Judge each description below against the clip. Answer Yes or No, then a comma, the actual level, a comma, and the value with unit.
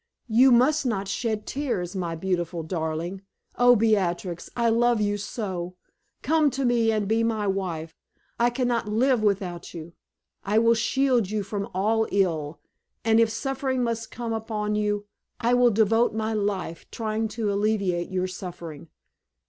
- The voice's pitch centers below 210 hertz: No, high, 215 Hz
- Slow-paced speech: No, average, 155 wpm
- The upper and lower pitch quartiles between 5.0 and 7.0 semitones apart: No, average, 3.8 semitones